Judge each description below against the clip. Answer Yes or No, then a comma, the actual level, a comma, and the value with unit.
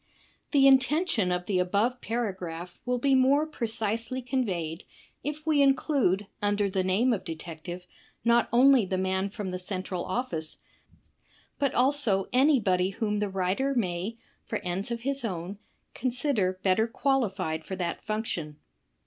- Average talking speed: Yes, average, 150 wpm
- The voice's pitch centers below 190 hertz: No, high, 210 Hz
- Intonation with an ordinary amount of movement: No, wide, 5.7 semitones